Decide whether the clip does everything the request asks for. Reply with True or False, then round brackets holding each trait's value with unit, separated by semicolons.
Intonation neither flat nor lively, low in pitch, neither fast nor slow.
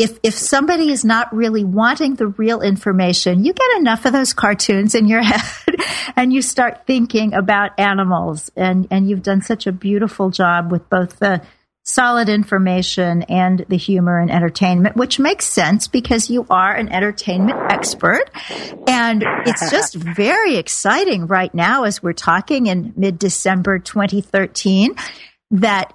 False (4.1 semitones; 205 Hz; 155 wpm)